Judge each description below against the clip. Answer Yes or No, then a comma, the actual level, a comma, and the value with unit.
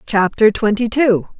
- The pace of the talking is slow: Yes, slow, 130 wpm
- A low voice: No, high, 220 Hz